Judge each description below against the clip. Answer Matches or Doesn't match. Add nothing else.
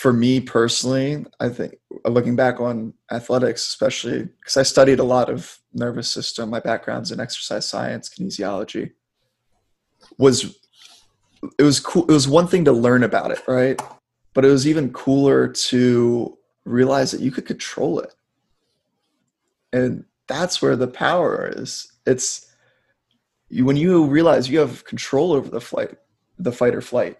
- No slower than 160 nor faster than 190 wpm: Doesn't match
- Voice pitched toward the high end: Doesn't match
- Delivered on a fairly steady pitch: Matches